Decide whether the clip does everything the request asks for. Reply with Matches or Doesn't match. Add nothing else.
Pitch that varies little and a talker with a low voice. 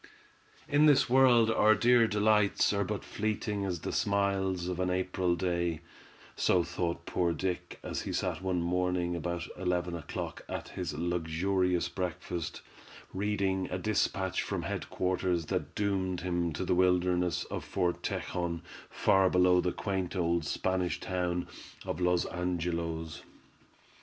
Matches